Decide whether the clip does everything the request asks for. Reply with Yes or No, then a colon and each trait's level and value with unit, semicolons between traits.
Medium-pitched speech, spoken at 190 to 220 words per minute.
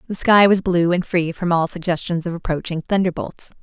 Yes: medium, 175 Hz; average, 200 wpm